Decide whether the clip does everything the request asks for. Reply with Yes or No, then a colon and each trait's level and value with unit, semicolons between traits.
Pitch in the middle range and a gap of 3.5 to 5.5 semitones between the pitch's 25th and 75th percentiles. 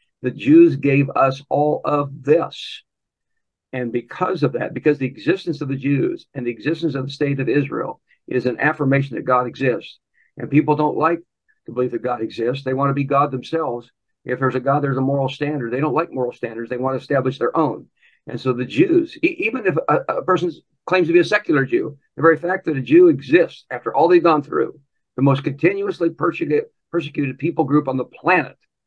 Yes: medium, 145 Hz; average, 4.1 semitones